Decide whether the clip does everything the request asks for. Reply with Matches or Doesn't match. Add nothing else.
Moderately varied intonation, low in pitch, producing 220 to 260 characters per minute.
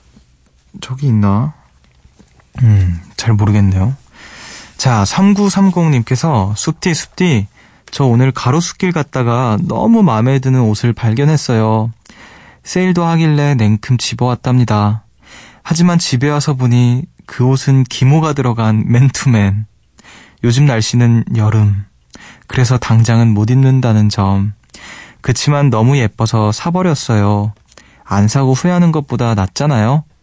Matches